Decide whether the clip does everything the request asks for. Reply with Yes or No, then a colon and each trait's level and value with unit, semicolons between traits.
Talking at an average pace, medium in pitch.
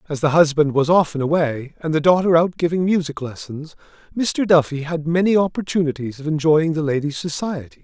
Yes: average, 175 wpm; medium, 160 Hz